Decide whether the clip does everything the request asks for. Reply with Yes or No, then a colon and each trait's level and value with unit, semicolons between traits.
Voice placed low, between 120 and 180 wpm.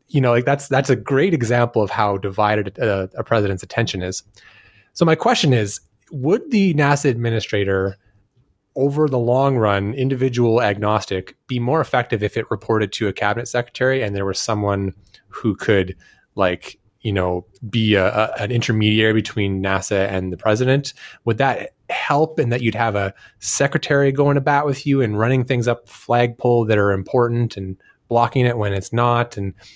Yes: low, 115 Hz; average, 175 wpm